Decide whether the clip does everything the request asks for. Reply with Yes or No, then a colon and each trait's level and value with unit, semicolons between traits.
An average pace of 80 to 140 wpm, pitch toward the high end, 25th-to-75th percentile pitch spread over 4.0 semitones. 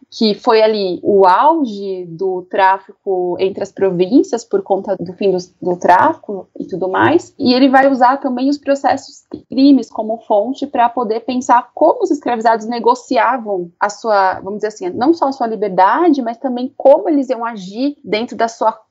No: average, 180 wpm; high, 230 Hz; wide, 5.4 semitones